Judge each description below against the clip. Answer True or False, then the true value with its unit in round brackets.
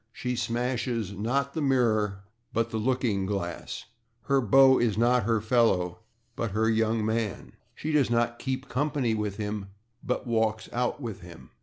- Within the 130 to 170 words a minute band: True (160 wpm)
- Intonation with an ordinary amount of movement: True (3.0 semitones)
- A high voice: False (115 Hz)